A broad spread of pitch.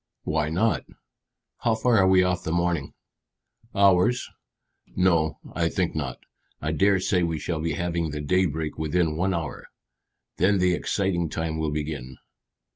No: average, 3.0 semitones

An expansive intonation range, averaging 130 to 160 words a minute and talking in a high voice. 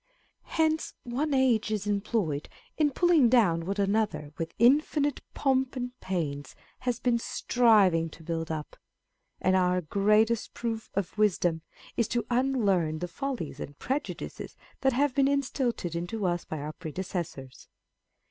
Yes: wide, 6.9 semitones; average, 145 wpm; high, 210 Hz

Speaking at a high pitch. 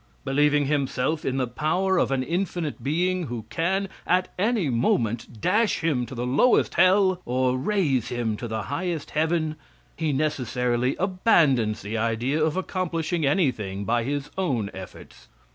No: medium, 145 Hz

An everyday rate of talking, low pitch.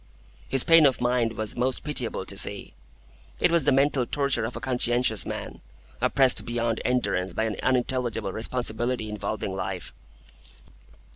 Yes: average, 145 wpm; low, 120 Hz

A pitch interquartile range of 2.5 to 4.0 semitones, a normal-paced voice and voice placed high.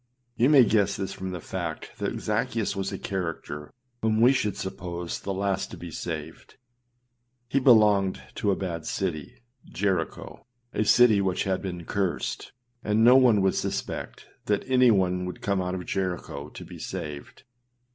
No: average, 3.0 semitones; average, 170 wpm; very low, 95 Hz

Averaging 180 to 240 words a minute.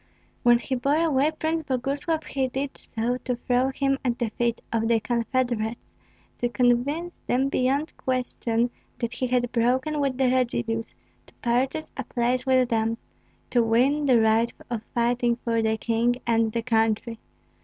No: average, 165 wpm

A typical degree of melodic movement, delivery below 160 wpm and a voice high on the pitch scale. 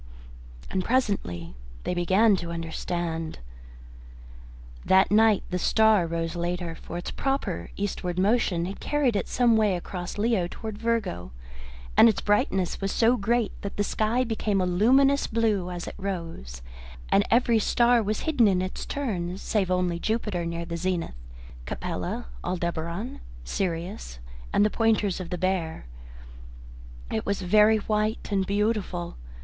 Yes: average, 4.1 semitones; average, 145 wpm; high, 195 Hz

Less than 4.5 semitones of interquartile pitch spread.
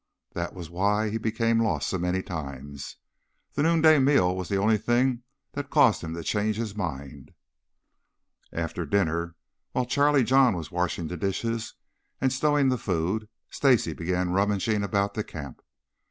No: wide, 5.5 semitones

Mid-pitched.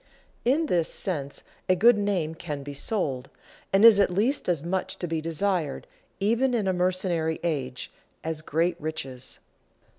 Yes: medium, 175 Hz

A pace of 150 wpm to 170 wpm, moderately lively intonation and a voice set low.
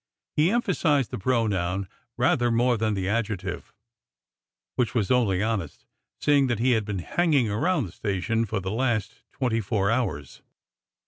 Yes: average, 165 wpm; average, 4.3 semitones; low, 115 Hz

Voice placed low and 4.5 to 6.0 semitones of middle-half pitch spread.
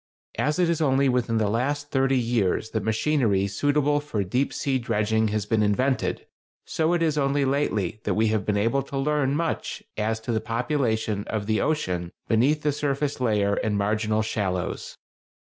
Yes: low, 115 Hz; average, 5.0 semitones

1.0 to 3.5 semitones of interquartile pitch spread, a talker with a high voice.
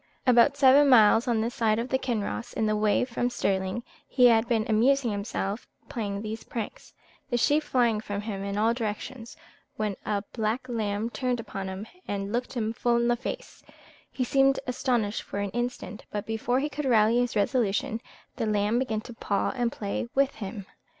Yes: average, 2.8 semitones; high, 230 Hz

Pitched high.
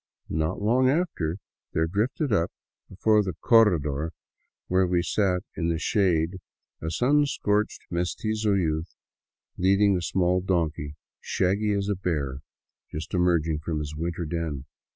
No: very low, 90 Hz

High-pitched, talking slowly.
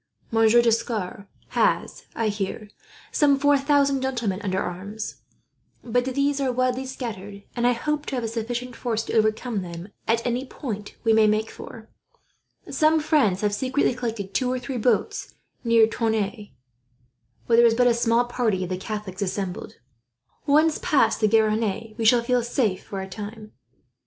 No: high, 230 Hz; average, 165 wpm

